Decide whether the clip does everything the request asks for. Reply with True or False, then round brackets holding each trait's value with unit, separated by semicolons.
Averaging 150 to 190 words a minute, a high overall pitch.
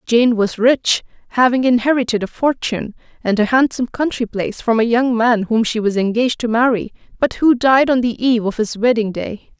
False (200 wpm; 235 Hz)